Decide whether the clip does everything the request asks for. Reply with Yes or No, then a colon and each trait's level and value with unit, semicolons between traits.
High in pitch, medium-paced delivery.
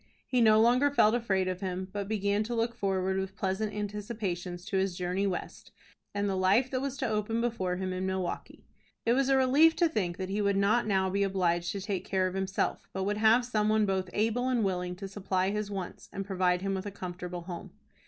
No: high, 195 Hz; fast, 225 wpm